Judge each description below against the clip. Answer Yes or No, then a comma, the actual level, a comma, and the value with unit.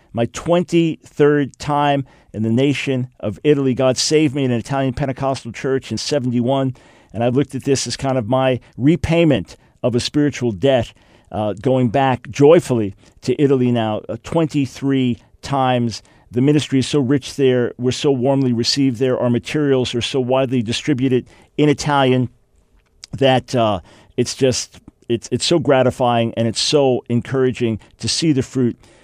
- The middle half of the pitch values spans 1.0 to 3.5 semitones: Yes, average, 2.7 semitones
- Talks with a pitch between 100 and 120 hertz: No, low, 130 Hz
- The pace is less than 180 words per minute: Yes, average, 160 wpm